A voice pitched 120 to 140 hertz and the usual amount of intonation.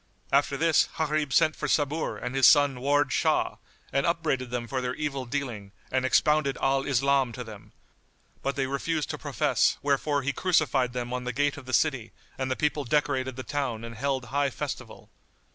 No: low, 135 Hz; narrow, 2.2 semitones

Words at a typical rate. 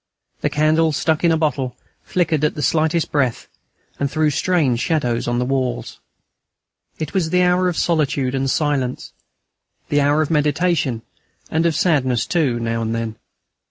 Yes: average, 160 wpm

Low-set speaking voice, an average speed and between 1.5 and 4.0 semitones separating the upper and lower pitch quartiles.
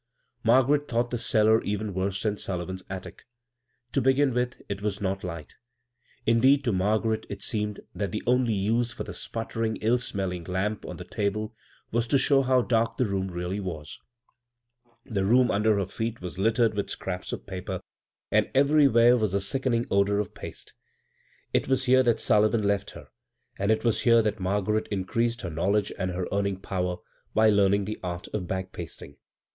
Yes: low, 105 Hz; average, 185 wpm; average, 3.5 semitones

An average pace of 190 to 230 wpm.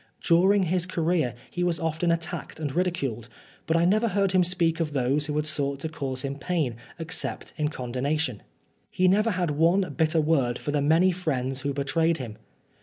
Yes: average, 200 wpm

